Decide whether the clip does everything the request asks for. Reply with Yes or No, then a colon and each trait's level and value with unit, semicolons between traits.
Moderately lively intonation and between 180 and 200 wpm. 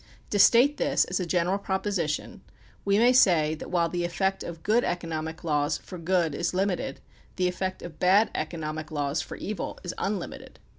Yes: average, 3.3 semitones; average, 185 wpm